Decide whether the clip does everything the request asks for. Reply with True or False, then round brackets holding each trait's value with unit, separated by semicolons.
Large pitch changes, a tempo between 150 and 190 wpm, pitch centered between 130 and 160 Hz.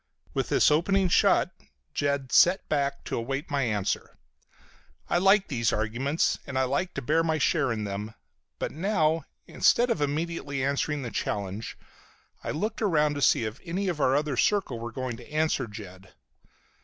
True (5.7 semitones; 170 wpm; 140 Hz)